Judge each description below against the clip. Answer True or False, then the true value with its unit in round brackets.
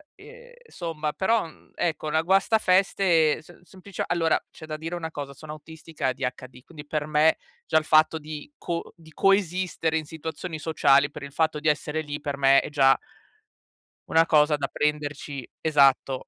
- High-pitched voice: False (155 Hz)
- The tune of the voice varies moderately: False (2.3 semitones)